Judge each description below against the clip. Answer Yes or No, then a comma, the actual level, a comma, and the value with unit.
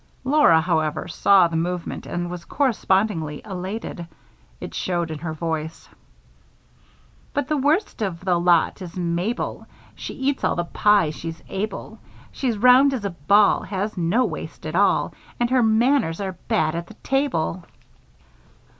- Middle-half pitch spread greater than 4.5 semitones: Yes, average, 5.3 semitones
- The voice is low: No, medium, 185 Hz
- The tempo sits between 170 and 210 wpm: No, average, 150 wpm